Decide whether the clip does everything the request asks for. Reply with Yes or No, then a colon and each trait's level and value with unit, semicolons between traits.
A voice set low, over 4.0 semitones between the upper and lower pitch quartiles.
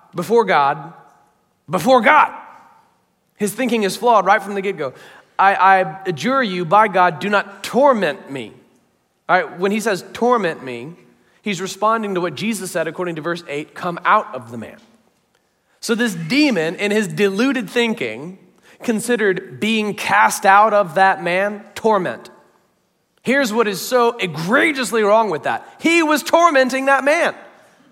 No: high, 205 Hz; average, 4.6 semitones